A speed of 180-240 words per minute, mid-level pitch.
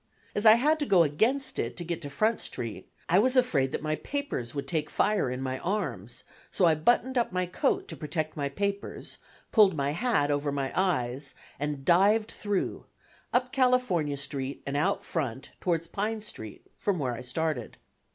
Yes: average, 185 wpm; medium, 165 Hz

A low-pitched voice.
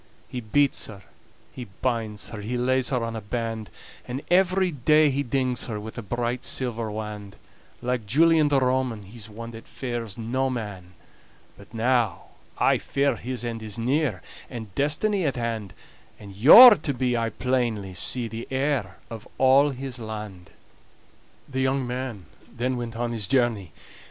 Yes: low, 120 Hz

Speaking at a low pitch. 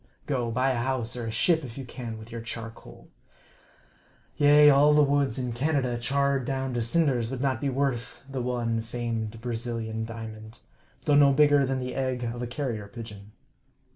Yes: low, 125 Hz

